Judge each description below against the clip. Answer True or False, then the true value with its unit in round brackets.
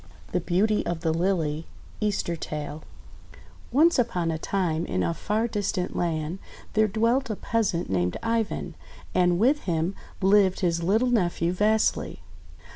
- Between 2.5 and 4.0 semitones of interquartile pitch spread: False (4.6 semitones)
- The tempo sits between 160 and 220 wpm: False (140 wpm)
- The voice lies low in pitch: False (185 Hz)